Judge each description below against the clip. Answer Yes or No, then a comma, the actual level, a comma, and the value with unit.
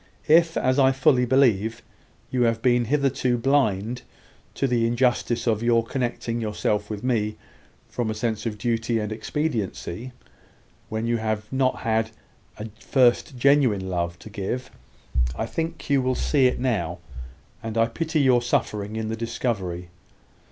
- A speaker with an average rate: Yes, average, 150 wpm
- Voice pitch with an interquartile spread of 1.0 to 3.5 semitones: Yes, average, 3.0 semitones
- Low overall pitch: Yes, low, 115 Hz